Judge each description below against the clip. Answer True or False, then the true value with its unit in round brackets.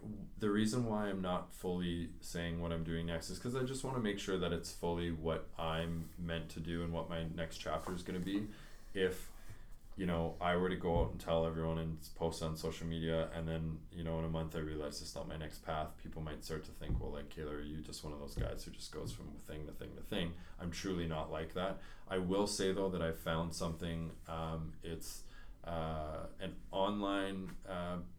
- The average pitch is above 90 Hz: False (85 Hz)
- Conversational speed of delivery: False (230 wpm)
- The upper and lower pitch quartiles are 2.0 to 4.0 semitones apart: True (2.4 semitones)